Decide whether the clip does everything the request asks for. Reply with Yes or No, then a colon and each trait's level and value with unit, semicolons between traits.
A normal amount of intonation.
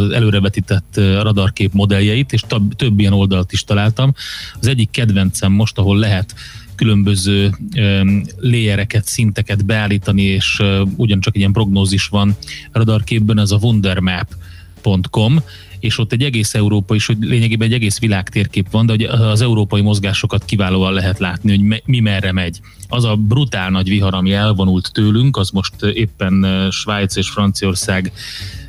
No: narrow, 2.2 semitones